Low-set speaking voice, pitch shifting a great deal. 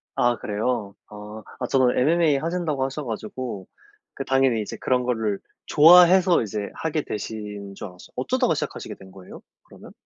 Yes: low, 125 Hz; wide, 6.0 semitones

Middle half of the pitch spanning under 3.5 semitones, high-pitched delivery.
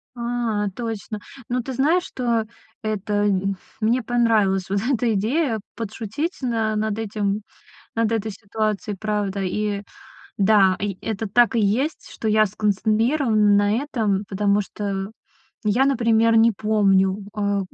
Yes: narrow, 2.4 semitones; high, 215 Hz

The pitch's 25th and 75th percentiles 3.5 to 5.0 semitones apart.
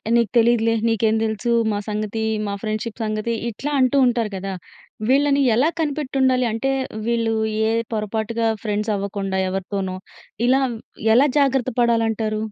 No: average, 2.9 semitones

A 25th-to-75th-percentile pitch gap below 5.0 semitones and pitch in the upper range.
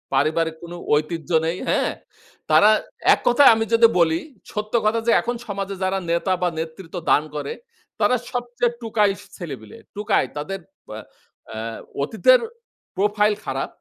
No: average, 5.3 semitones; high, 195 Hz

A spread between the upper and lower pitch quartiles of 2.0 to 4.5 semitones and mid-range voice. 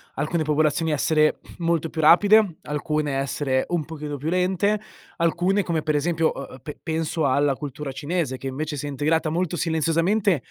Yes: narrow, 2.6 semitones; medium, 155 Hz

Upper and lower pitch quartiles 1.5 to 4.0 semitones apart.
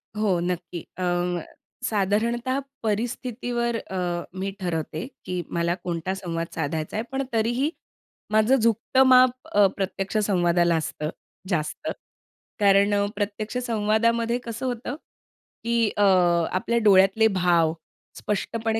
No: average, 4.6 semitones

